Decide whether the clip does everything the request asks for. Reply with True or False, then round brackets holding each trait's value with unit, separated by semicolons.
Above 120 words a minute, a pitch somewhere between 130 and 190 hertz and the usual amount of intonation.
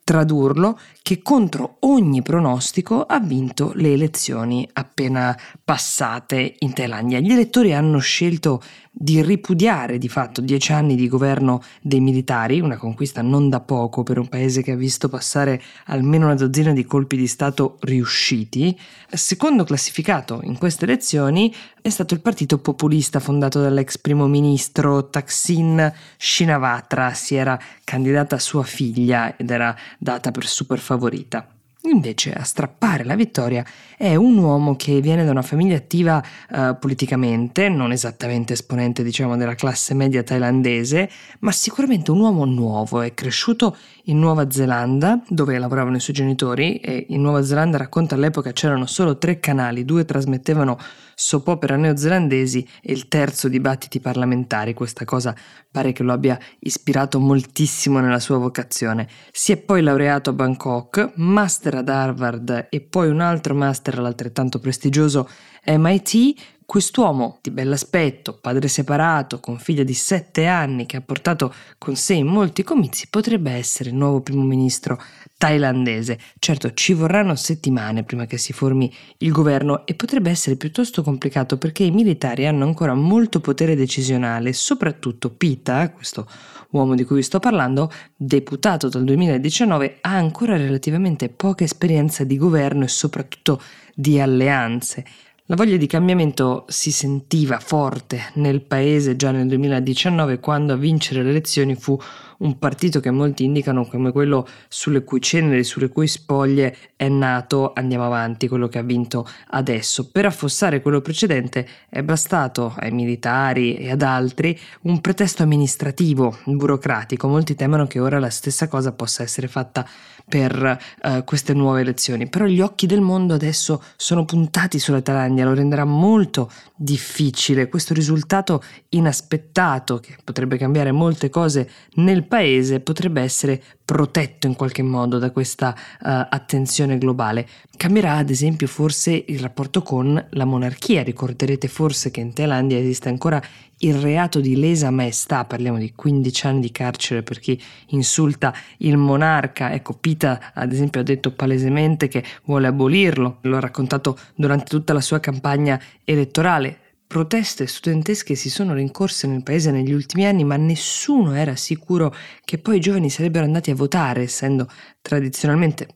True (150 wpm; 140 Hz; 3.6 semitones)